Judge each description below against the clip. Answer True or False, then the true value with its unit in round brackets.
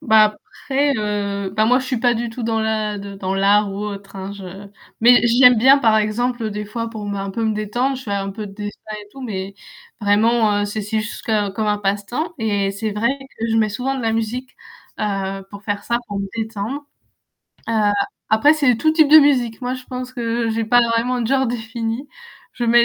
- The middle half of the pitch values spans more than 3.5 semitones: False (2.9 semitones)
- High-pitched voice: True (220 Hz)